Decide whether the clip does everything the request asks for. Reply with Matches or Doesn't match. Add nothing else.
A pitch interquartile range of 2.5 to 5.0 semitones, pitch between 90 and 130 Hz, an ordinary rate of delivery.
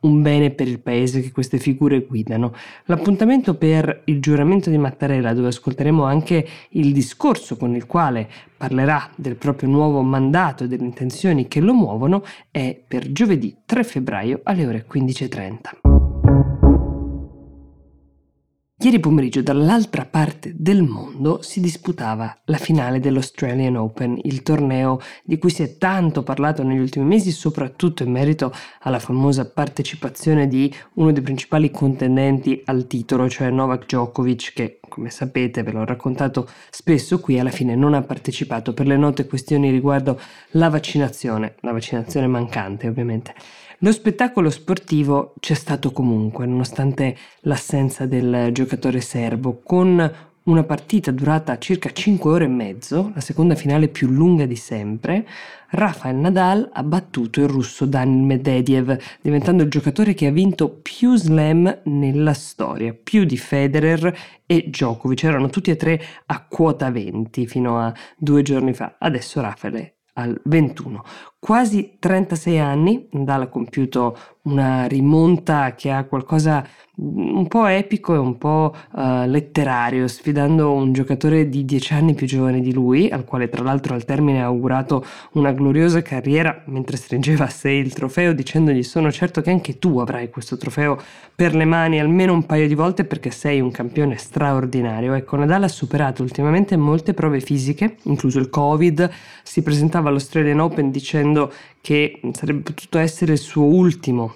Doesn't match